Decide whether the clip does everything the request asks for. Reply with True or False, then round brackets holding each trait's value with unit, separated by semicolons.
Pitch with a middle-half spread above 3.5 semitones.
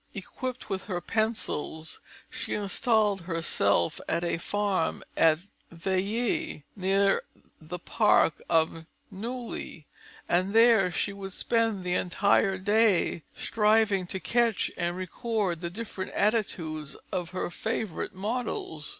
True (4.1 semitones)